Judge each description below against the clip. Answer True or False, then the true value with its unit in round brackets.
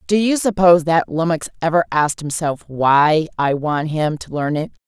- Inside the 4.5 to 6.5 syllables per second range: True (5.0 syllables/s)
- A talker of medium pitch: True (160 Hz)